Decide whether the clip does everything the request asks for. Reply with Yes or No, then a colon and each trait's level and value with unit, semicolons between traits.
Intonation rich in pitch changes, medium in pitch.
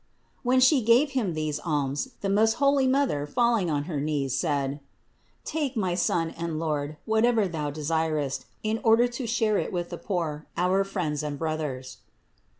Yes: wide, 7.3 semitones; medium, 175 Hz